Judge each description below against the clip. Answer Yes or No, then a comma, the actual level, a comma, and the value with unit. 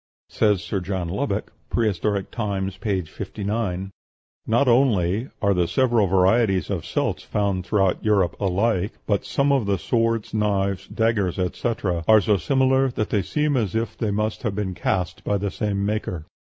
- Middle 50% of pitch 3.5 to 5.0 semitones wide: No, average, 3.1 semitones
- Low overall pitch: Yes, low, 100 Hz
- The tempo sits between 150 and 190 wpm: Yes, average, 165 wpm